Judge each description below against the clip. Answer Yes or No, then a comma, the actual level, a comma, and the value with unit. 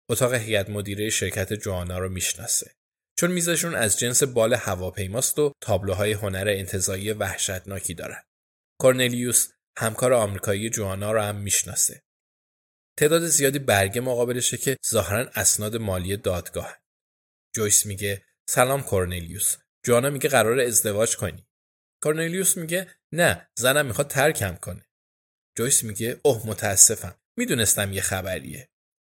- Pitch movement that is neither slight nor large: Yes, average, 4.7 semitones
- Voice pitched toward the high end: No, low, 105 Hz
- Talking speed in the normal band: Yes, average, 120 wpm